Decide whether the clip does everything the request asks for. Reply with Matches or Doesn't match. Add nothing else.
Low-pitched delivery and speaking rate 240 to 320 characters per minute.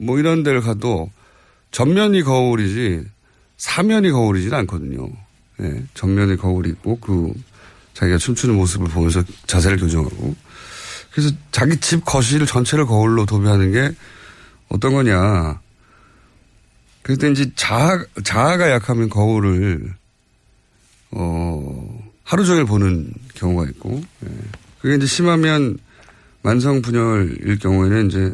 Matches